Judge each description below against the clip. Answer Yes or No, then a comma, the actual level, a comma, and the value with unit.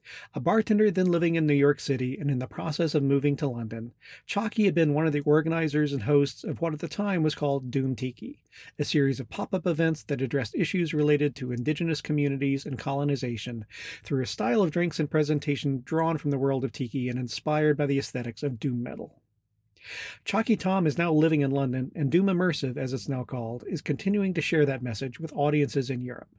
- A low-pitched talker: No, medium, 145 Hz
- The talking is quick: Yes, fast, 215 wpm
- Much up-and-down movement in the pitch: No, average, 3.4 semitones